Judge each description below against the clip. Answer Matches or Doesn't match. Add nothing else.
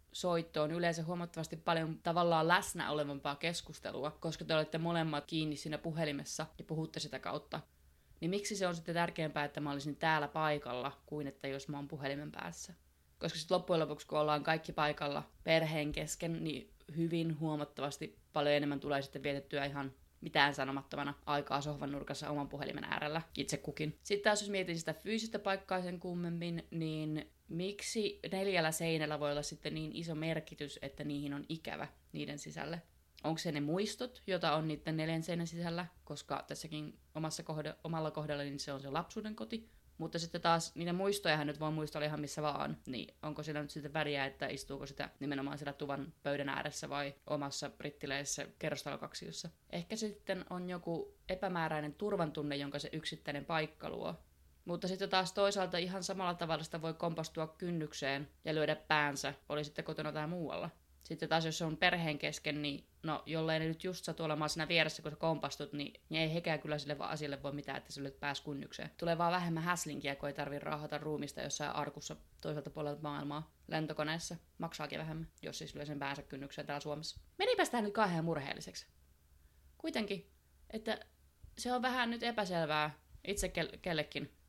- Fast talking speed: Matches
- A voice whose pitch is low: Doesn't match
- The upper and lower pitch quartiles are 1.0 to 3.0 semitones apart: Matches